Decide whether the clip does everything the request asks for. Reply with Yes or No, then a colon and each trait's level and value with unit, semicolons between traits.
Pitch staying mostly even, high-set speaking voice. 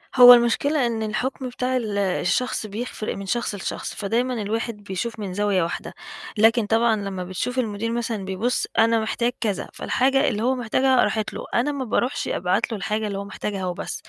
No: average, 3.4 semitones; high, 225 Hz